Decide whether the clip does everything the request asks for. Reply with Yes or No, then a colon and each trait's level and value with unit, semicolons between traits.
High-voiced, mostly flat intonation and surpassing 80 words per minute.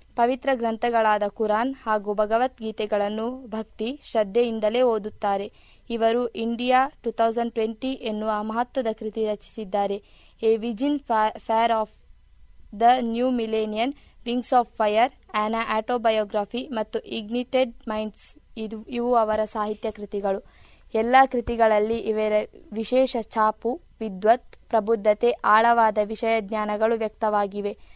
Yes: high, 225 Hz; narrow, 1.8 semitones; fast, 105 wpm